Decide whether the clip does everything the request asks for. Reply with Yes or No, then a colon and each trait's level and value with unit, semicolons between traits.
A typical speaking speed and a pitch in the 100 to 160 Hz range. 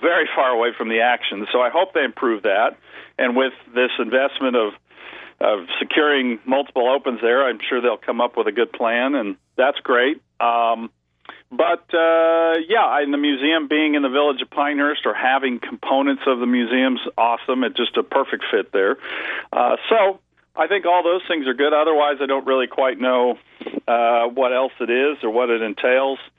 Yes: average, 195 wpm; low, 135 Hz